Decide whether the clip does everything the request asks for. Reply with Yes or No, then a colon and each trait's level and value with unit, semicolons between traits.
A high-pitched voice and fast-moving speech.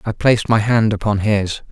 No: low, 105 Hz; fast, 210 wpm